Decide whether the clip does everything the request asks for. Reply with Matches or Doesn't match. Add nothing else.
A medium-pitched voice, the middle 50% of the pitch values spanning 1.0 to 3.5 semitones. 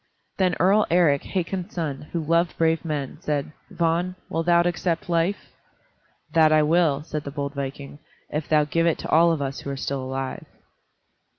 Matches